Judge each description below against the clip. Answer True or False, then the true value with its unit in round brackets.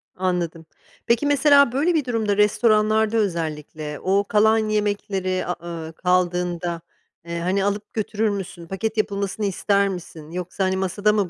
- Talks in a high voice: True (200 Hz)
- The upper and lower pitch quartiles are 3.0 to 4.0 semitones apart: True (3.3 semitones)